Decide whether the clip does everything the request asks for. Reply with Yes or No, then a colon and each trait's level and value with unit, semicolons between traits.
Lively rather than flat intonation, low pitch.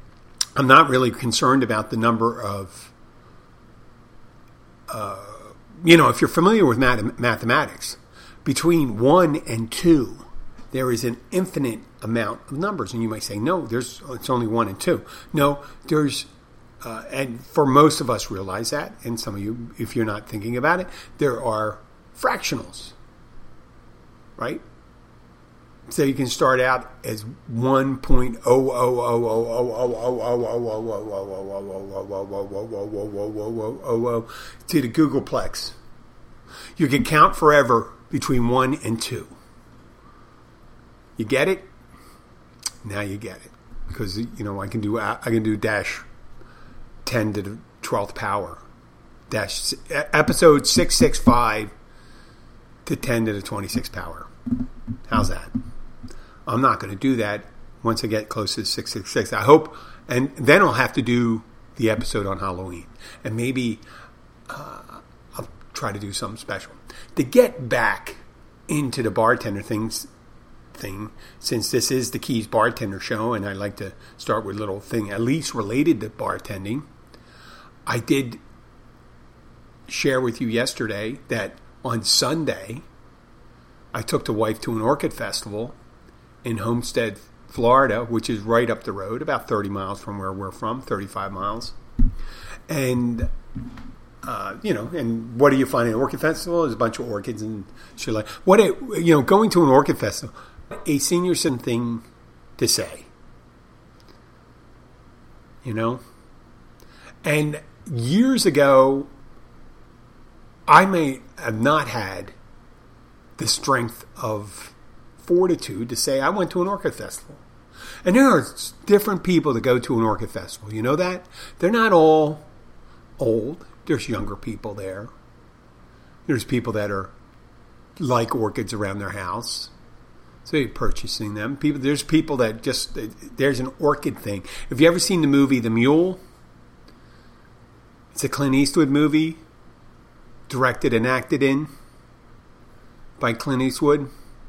No: average, 4.2 semitones; low, 120 Hz